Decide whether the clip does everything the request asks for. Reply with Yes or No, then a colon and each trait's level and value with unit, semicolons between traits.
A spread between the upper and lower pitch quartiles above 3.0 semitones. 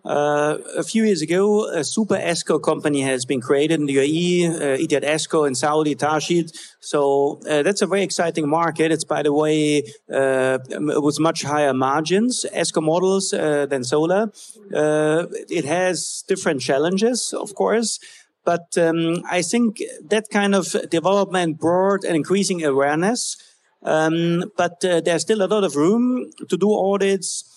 Yes: average, 4.6 semitones